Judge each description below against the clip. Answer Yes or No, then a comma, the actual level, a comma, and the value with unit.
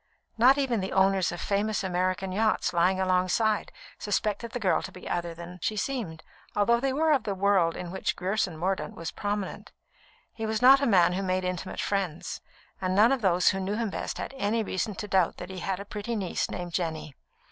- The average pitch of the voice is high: Yes, high, 195 Hz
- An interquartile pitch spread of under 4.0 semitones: Yes, average, 3.0 semitones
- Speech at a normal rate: No, fast, 210 wpm